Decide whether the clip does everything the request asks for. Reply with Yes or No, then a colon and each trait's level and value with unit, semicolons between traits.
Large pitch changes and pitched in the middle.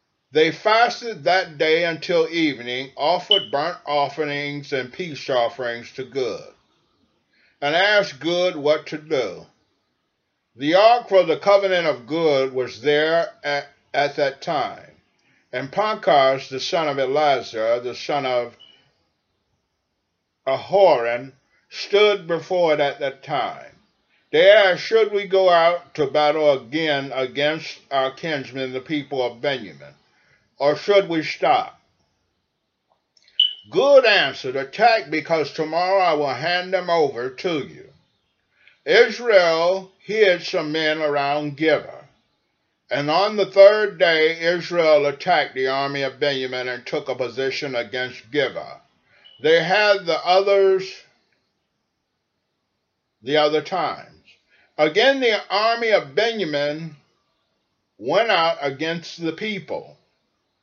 Yes: wide, 5.7 semitones; medium, 155 Hz